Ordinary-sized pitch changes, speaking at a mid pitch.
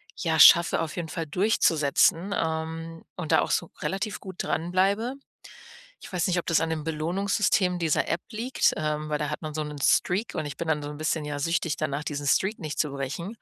Yes: average, 3.1 semitones; medium, 165 Hz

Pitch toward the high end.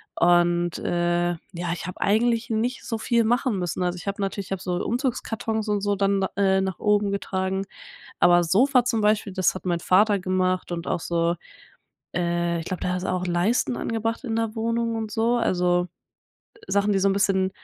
Yes: high, 195 Hz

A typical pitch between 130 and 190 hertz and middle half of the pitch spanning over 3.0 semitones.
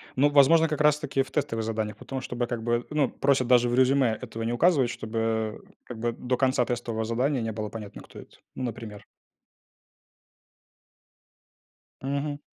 No: low, 120 Hz; average, 3.5 semitones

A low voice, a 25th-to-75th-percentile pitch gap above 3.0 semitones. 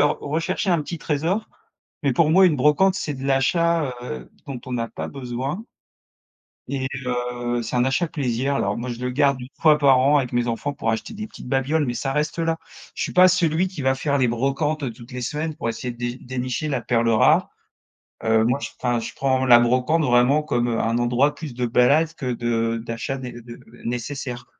Yes: low, 130 Hz; average, 3.7 semitones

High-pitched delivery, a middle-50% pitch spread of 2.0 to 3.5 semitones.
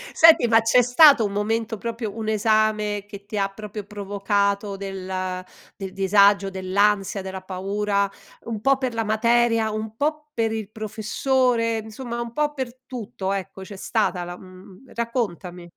Yes: high, 215 Hz; average, 2.8 semitones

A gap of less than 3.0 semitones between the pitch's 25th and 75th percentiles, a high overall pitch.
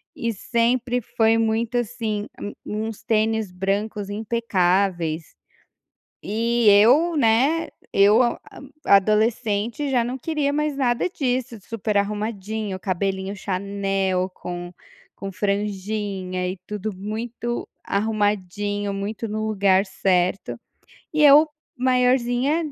No: average, 3.3 semitones; high, 215 Hz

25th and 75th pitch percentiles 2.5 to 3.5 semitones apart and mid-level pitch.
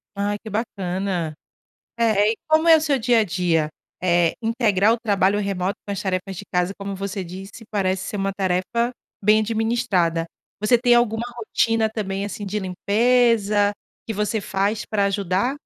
No: average, 2.9 semitones; high, 205 Hz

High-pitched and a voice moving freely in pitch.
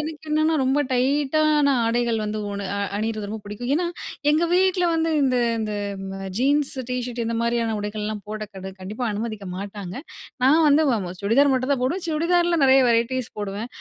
Yes: very high, 250 Hz; wide, 5.7 semitones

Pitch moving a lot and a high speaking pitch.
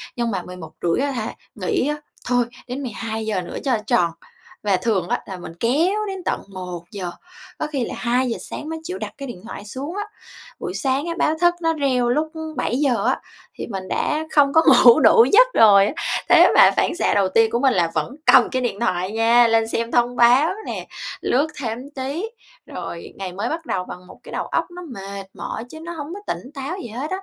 Yes: wide, 6.2 semitones; high, 245 Hz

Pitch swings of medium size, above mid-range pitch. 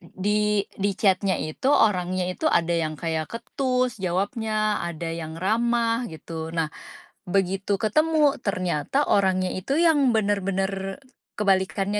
Yes: average, 3.4 semitones; high, 195 Hz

